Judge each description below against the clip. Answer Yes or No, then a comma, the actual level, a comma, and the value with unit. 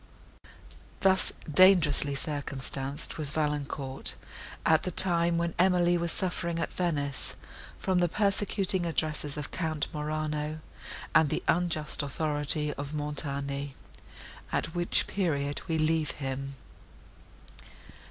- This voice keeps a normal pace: No, slow, 110 wpm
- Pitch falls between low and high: Yes, medium, 155 Hz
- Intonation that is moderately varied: Yes, average, 3.2 semitones